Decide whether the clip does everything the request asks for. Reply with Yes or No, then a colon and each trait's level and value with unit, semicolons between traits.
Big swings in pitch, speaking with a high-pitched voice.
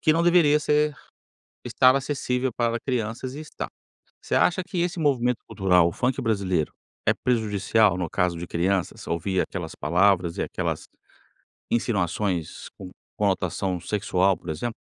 No: wide, 6.1 semitones; low, 105 Hz